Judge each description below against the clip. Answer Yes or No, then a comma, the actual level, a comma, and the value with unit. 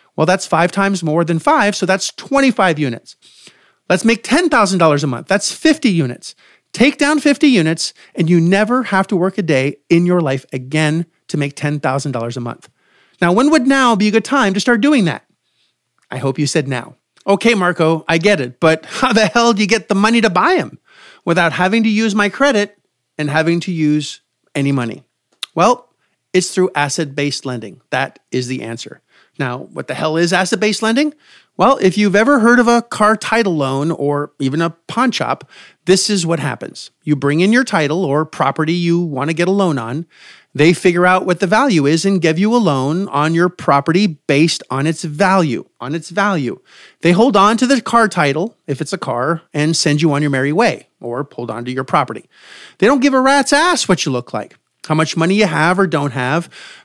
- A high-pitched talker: No, medium, 170 Hz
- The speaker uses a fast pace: Yes, fast, 210 wpm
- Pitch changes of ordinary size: No, wide, 5.8 semitones